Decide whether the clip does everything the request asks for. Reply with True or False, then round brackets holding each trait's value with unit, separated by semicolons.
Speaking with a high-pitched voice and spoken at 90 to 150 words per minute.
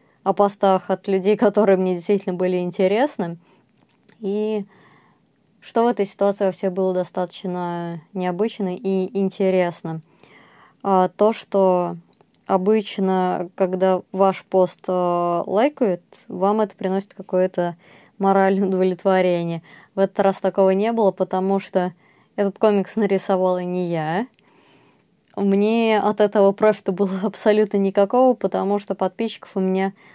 True (195 Hz; 115 wpm)